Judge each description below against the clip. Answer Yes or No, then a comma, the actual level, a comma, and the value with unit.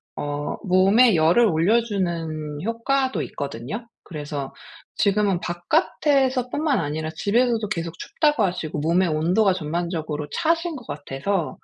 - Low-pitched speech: No, medium, 185 Hz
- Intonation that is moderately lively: No, wide, 6.9 semitones